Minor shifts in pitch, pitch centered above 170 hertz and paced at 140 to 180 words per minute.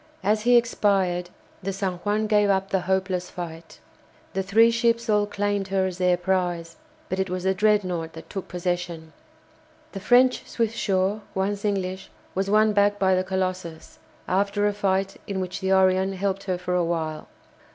Yes: narrow, 2.0 semitones; high, 190 Hz; average, 170 wpm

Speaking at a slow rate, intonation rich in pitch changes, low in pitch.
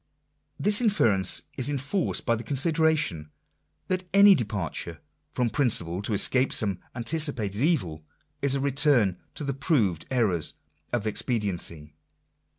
Yes: slow, 130 wpm; wide, 6.9 semitones; low, 120 Hz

